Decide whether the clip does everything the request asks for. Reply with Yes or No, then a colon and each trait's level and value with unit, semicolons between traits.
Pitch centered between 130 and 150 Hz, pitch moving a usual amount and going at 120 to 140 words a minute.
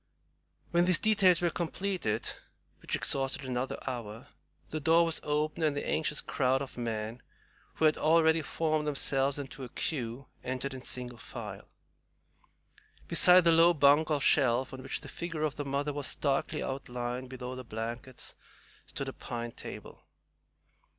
No: medium, 140 Hz; average, 3.9 semitones; average, 155 wpm